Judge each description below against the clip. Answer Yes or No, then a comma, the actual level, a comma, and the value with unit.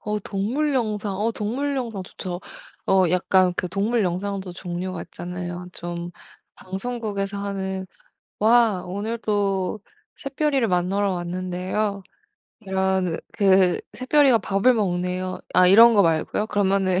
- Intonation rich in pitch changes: No, average, 2.9 semitones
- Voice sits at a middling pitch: No, high, 195 Hz